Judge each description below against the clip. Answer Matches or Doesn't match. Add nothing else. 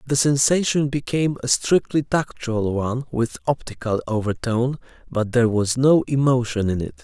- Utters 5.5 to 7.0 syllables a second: Doesn't match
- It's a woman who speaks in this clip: Doesn't match